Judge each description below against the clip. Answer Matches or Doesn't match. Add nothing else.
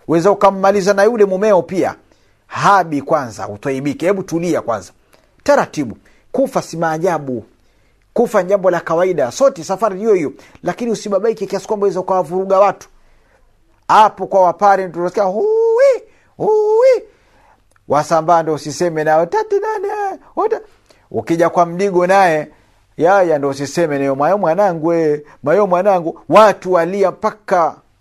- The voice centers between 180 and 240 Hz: Matches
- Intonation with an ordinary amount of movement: Matches